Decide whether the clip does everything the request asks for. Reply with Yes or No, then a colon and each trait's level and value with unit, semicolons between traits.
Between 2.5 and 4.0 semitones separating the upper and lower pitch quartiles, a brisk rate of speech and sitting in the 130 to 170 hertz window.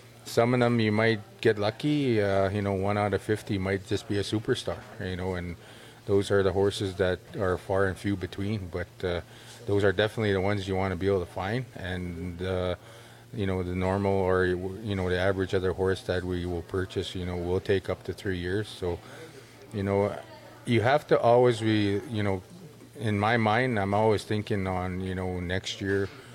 No: average, 2.9 semitones; fast, 210 wpm; low, 100 Hz